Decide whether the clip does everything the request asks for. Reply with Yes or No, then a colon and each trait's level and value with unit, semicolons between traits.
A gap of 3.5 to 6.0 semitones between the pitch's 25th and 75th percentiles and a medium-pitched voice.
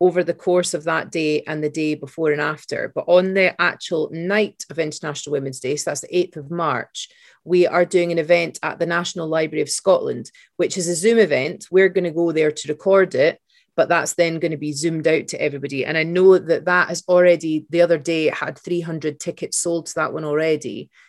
No: narrow, 2.4 semitones; medium, 170 Hz